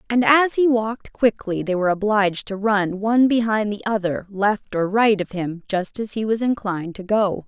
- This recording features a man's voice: No, female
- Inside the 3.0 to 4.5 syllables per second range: No, 5.1 syllables/s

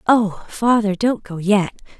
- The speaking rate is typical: Yes, average, 150 wpm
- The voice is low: No, high, 210 Hz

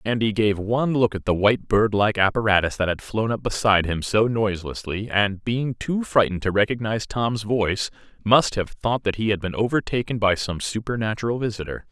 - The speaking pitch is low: Yes, low, 110 Hz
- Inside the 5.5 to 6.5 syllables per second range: Yes, 5.6 syllables/s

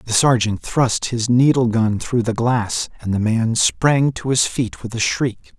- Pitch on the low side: Yes, low, 120 Hz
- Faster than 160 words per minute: Yes, fast, 205 wpm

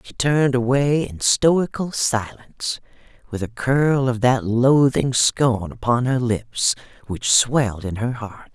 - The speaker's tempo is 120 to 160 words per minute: Yes, average, 150 wpm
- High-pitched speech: No, low, 125 Hz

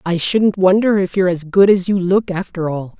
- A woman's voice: Yes, female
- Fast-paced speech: Yes, fast, 240 wpm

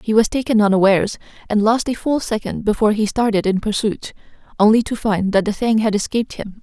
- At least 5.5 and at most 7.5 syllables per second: Yes, 6.0 syllables/s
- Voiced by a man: No, female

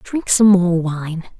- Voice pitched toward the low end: No, medium, 185 Hz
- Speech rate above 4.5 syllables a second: No, 3.3 syllables/s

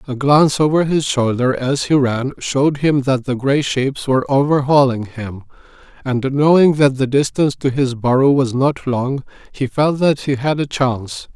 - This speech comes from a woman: No, male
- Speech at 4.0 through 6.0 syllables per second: Yes, 4.9 syllables/s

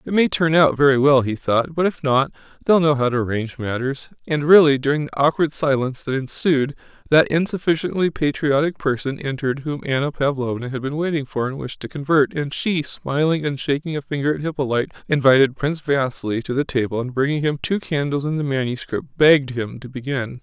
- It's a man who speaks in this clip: Yes, male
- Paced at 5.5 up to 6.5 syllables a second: Yes, 5.8 syllables/s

